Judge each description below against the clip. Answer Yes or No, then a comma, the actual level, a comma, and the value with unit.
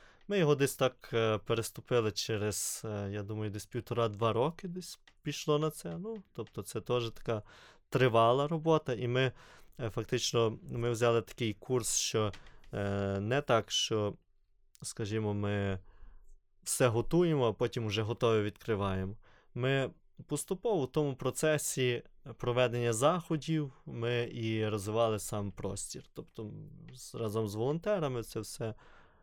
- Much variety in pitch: No, average, 4.2 semitones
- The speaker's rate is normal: Yes, average, 125 wpm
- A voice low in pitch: Yes, low, 115 Hz